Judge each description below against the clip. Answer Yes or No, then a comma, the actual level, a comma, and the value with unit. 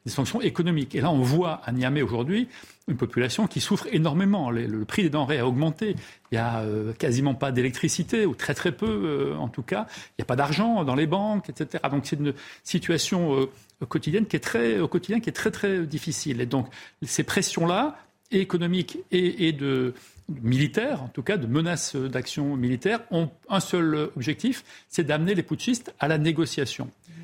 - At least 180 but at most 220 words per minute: Yes, average, 185 wpm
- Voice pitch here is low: No, medium, 155 Hz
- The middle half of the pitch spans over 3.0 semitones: Yes, average, 5.2 semitones